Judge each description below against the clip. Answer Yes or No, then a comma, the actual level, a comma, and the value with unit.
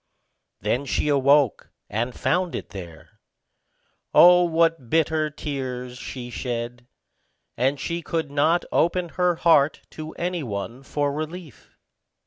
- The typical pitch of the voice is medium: Yes, medium, 145 Hz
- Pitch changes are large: No, average, 4.8 semitones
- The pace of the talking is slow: Yes, slow, 120 wpm